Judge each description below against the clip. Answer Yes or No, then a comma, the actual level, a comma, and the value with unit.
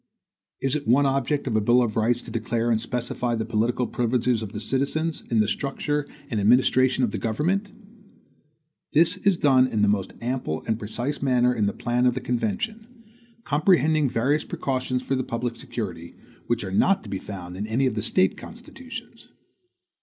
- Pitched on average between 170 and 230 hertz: No, low, 125 Hz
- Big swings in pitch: No, average, 3.8 semitones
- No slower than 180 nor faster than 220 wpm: Yes, average, 185 wpm